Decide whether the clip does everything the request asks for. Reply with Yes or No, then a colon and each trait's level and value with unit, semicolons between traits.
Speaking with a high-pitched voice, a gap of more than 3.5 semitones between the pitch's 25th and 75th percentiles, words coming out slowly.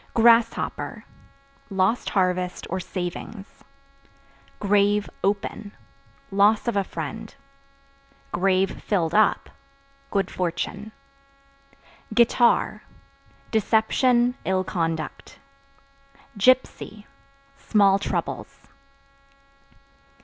No: high, 200 Hz; average, 2.9 semitones; slow, 65 wpm